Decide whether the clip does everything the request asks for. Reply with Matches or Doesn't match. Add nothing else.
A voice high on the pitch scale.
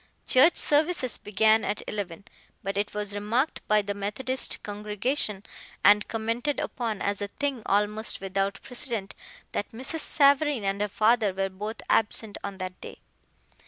Matches